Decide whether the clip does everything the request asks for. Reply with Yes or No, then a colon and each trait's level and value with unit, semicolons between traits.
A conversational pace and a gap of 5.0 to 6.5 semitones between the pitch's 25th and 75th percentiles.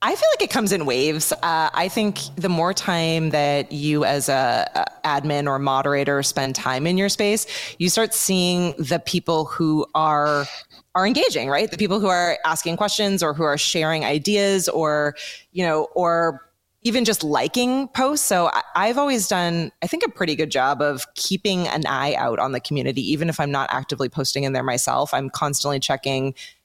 Yes: average, 195 wpm; average, 5.3 semitones